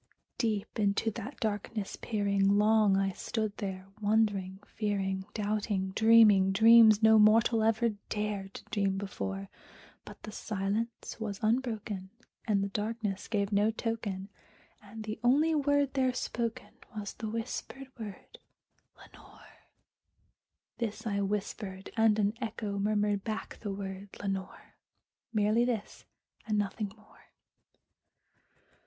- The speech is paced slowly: Yes, slow, 125 wpm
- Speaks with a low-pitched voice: No, high, 210 Hz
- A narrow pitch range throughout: Yes, narrow, 2.0 semitones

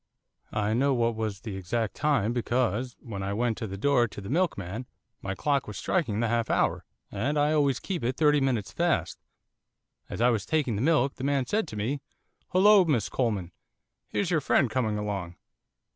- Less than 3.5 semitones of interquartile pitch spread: No, average, 5.2 semitones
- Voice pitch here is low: Yes, low, 120 Hz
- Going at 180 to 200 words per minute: Yes, average, 190 wpm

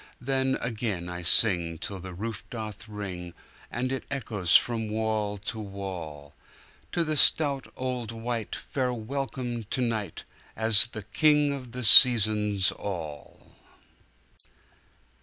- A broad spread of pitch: No, average, 4.2 semitones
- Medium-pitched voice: No, low, 110 Hz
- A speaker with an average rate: No, slow, 115 wpm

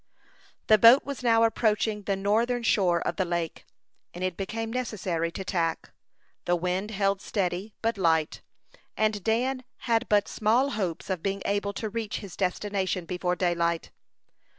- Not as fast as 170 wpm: Yes, average, 155 wpm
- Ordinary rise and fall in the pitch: Yes, average, 3.7 semitones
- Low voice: No, high, 200 Hz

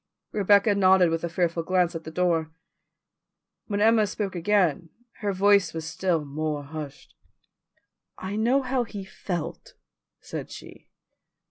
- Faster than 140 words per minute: No, slow, 135 wpm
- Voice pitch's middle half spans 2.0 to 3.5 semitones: No, average, 3.9 semitones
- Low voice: No, medium, 185 Hz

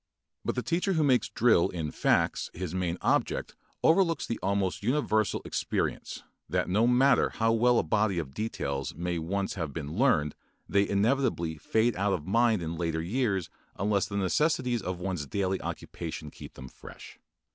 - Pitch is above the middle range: No, low, 100 Hz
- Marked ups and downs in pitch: Yes, wide, 5.8 semitones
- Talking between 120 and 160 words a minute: No, average, 170 wpm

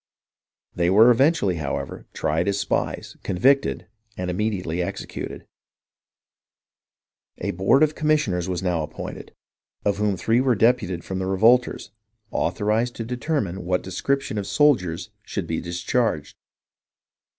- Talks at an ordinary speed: No, slow, 125 wpm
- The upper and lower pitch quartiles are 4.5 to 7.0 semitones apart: Yes, wide, 5.4 semitones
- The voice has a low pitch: Yes, low, 100 Hz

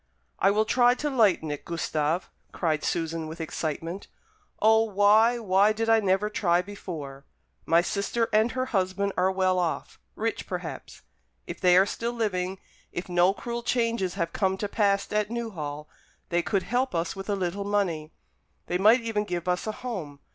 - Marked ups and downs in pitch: No, average, 3.9 semitones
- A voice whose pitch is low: No, high, 195 Hz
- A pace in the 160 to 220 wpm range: Yes, average, 175 wpm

